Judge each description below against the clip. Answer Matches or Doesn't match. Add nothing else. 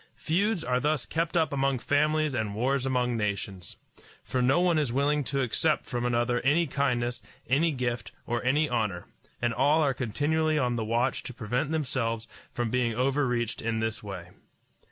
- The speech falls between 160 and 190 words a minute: Matches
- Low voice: Matches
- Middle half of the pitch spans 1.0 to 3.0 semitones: Doesn't match